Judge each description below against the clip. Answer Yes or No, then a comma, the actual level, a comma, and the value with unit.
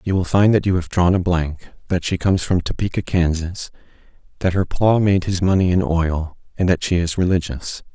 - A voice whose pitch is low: Yes, very low, 90 Hz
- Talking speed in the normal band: No, fast, 210 wpm